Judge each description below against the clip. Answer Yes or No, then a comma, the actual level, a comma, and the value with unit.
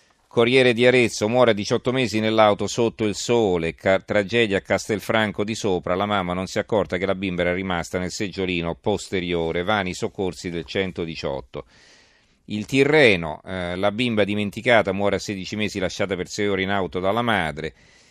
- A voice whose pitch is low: Yes, low, 100 Hz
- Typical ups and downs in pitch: Yes, average, 3.1 semitones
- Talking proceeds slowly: No, fast, 170 wpm